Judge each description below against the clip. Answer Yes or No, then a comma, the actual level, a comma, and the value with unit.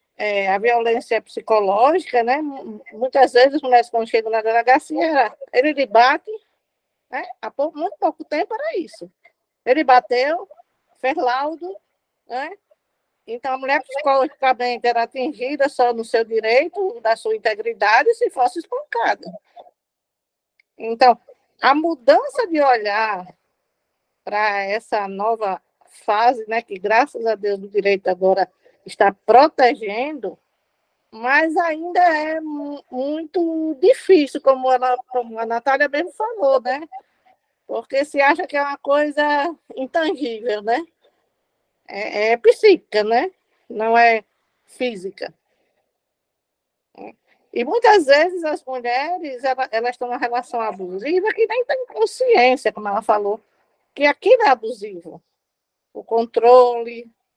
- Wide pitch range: Yes, wide, 6.0 semitones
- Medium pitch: No, very high, 260 Hz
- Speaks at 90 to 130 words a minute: Yes, average, 125 wpm